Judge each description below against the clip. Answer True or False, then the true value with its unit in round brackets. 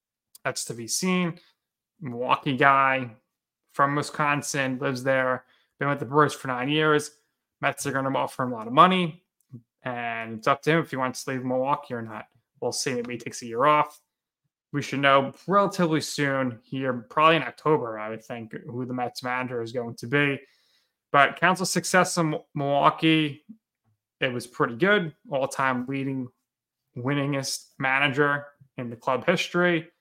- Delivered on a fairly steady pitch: False (3.3 semitones)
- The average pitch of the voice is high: False (140 Hz)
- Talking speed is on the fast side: False (170 wpm)